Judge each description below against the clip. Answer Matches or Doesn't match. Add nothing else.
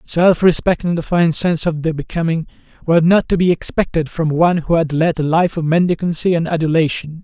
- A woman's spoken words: Doesn't match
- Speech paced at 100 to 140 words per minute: Doesn't match